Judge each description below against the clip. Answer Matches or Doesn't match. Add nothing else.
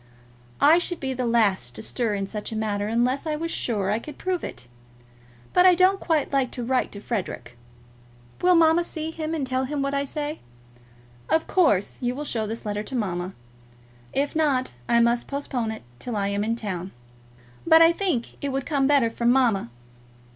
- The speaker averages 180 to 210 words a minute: Matches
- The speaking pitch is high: Matches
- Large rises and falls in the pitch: Matches